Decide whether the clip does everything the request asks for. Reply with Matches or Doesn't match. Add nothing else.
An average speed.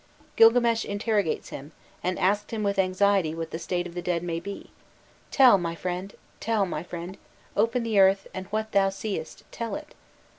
Matches